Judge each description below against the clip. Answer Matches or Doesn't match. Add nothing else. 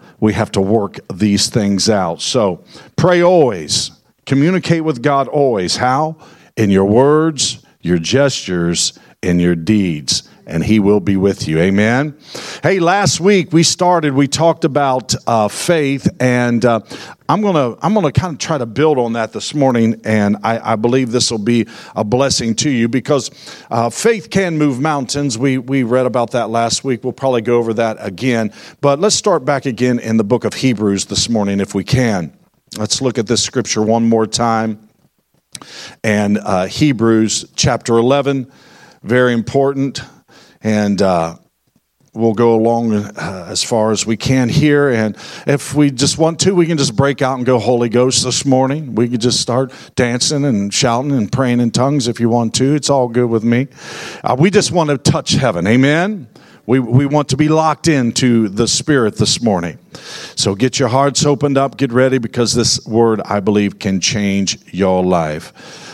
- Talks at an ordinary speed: Matches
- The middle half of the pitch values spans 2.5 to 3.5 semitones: Doesn't match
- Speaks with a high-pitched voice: Doesn't match